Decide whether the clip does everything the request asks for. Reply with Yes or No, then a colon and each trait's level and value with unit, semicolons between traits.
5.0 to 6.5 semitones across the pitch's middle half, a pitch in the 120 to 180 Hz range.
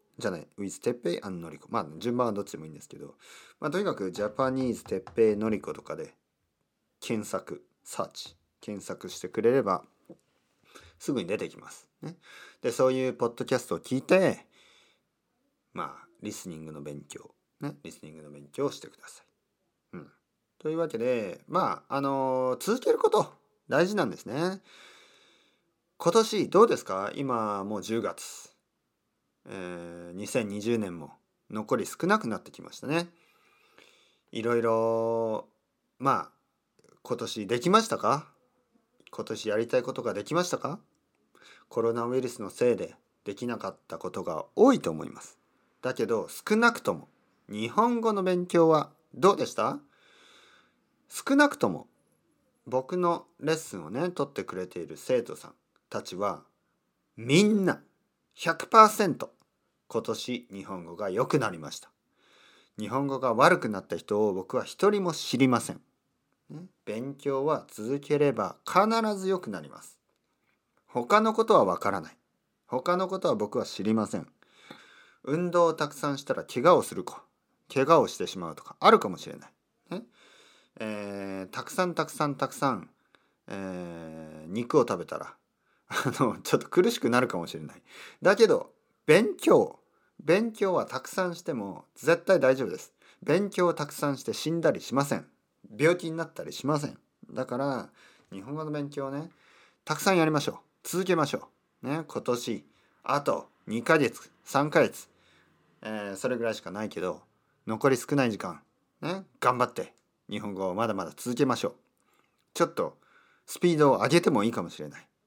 No: wide, 8.7 semitones; low, 135 Hz